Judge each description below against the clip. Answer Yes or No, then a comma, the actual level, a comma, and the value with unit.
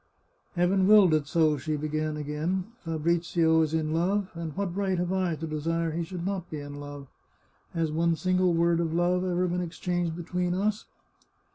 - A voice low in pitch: No, medium, 170 Hz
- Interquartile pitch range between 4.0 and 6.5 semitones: No, narrow, 2.5 semitones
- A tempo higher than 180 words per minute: Yes, average, 190 wpm